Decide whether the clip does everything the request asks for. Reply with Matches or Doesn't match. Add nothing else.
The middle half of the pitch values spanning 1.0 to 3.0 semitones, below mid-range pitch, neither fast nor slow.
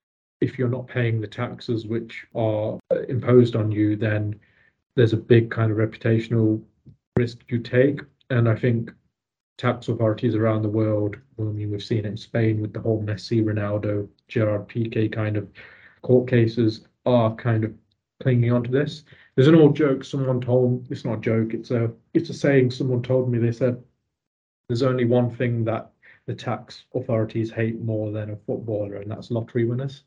Matches